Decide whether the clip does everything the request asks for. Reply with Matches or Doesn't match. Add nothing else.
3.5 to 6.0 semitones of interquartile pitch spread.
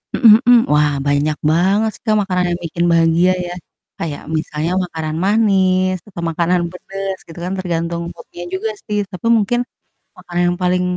Doesn't match